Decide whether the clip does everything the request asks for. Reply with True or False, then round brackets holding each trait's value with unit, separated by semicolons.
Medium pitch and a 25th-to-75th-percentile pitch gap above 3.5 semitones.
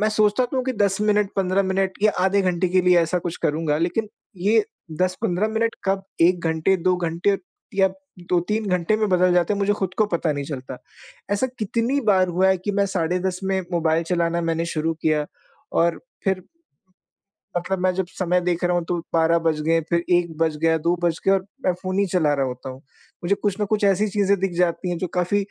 False (180 Hz; 3.0 semitones)